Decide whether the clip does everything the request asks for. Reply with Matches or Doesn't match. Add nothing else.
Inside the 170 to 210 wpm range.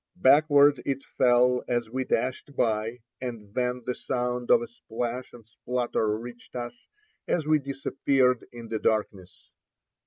Doesn't match